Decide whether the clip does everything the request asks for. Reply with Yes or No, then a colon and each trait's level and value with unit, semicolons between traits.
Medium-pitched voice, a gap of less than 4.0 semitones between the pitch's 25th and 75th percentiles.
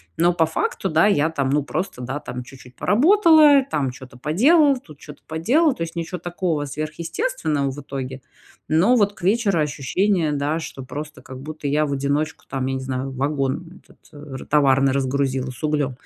No: medium, 150 Hz; average, 4.6 semitones